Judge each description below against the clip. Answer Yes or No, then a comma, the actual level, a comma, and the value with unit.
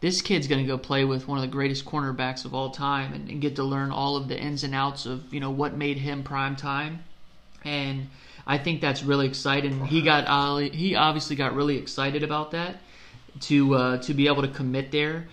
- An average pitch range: No, narrow, 1.4 semitones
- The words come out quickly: Yes, fast, 225 wpm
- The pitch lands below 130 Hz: No, medium, 140 Hz